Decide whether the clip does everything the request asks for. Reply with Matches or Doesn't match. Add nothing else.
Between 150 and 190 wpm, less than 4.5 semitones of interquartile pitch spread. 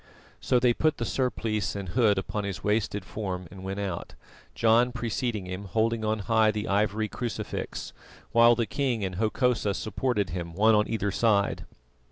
Matches